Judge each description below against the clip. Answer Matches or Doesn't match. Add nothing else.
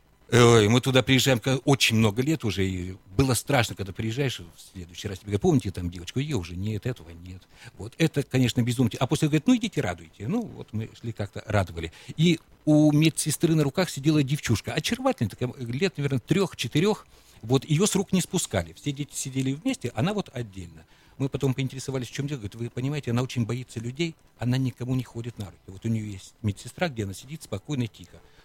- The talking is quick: Matches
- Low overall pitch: Matches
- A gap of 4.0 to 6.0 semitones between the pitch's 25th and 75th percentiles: Matches